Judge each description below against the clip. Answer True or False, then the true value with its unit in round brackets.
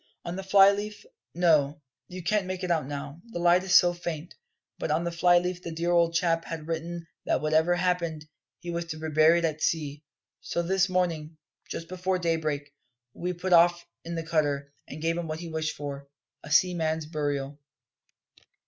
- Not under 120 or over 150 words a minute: False (190 wpm)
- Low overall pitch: False (170 Hz)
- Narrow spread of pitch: True (2.2 semitones)